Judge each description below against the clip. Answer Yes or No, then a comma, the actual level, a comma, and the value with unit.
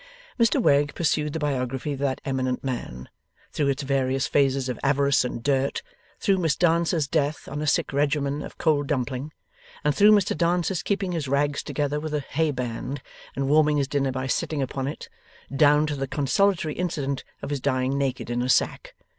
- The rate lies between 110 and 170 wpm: No, average, 185 wpm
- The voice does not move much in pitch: Yes, narrow, 2.3 semitones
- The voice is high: No, medium, 140 Hz